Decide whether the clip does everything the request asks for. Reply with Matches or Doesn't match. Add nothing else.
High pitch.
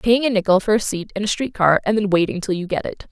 Matches